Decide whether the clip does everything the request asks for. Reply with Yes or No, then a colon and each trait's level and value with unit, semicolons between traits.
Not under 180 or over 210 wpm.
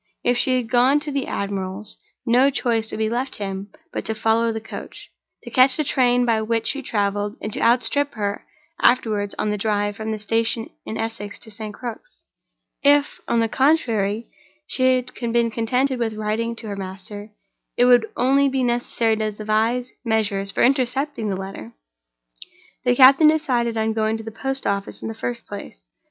Yes: average, 185 wpm